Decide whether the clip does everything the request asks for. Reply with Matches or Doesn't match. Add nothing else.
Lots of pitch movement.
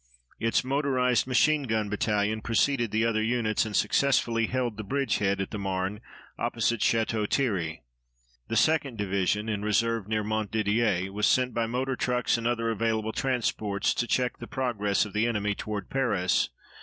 Doesn't match